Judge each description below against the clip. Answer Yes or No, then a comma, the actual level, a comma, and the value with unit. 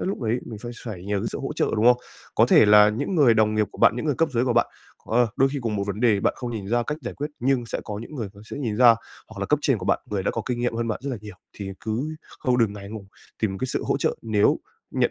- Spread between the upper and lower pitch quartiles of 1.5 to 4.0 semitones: Yes, average, 3.0 semitones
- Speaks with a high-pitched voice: No, low, 115 Hz